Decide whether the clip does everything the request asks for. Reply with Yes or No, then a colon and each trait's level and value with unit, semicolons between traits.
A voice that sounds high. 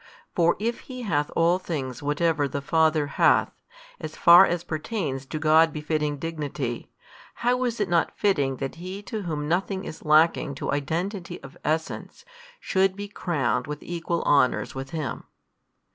No: medium, 160 Hz